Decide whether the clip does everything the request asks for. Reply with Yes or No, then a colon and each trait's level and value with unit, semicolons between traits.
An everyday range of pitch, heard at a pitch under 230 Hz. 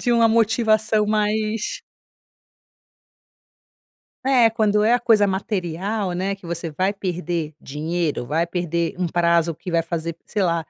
Yes: average, 4.2 semitones; medium, 185 Hz